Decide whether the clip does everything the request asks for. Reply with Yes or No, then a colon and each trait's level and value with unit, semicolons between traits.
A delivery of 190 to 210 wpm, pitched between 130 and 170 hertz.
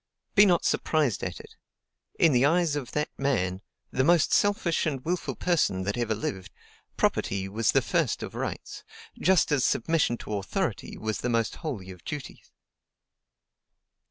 No: average, 155 wpm; low, 135 Hz